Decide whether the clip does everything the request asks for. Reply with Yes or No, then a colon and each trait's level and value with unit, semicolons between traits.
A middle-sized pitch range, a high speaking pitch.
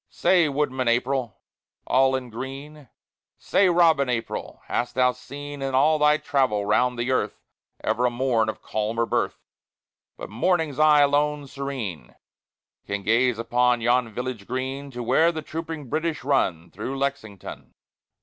No: average, 3.4 semitones; low, 130 Hz